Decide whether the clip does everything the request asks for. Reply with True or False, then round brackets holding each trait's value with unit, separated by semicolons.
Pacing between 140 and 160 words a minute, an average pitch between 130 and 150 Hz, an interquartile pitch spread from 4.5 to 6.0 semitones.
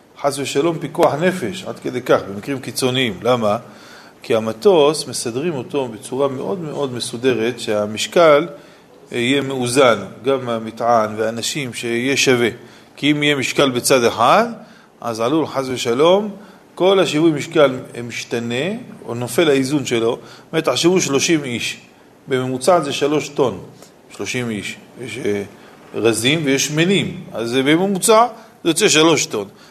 False (130 wpm; 135 Hz; 5.1 semitones)